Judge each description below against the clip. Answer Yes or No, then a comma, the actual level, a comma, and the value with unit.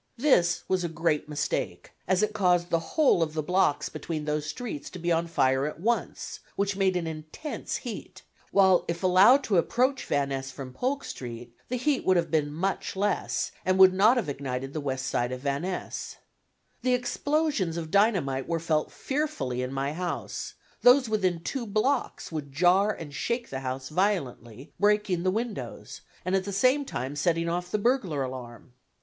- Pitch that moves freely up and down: Yes, wide, 6.4 semitones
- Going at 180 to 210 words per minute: Yes, average, 185 wpm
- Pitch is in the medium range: Yes, medium, 175 Hz